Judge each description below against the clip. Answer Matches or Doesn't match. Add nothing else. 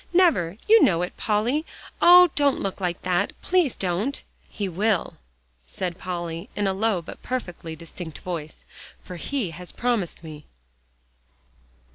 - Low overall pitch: Doesn't match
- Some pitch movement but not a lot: Doesn't match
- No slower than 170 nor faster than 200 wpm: Doesn't match